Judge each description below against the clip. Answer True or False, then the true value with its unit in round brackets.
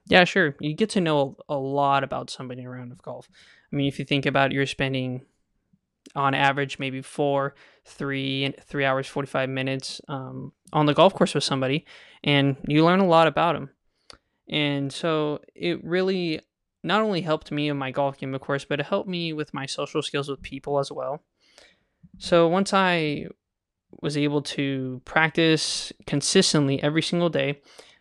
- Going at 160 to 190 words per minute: True (175 wpm)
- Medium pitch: True (145 Hz)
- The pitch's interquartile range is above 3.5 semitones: False (2.7 semitones)